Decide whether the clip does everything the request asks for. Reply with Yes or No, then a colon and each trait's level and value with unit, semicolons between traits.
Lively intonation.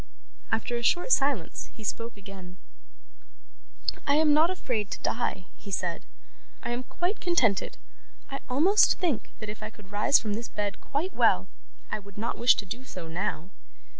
Yes: wide, 6.0 semitones